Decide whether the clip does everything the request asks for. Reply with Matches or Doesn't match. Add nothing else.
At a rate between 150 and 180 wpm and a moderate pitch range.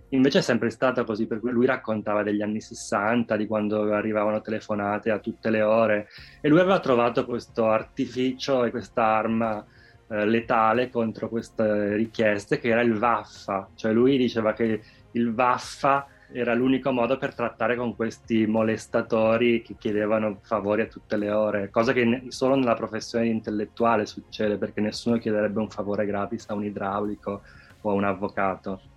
Doesn't match